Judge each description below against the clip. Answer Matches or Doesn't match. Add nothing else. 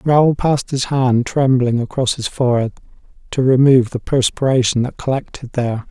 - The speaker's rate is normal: Matches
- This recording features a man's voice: Matches